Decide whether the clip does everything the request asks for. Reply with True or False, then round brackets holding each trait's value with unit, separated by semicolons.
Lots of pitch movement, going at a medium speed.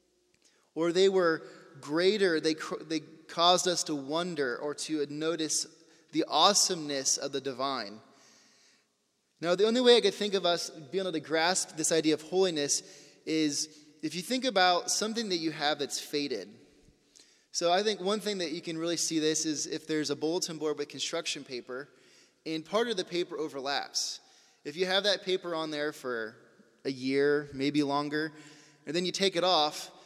False (3.4 semitones; 180 wpm)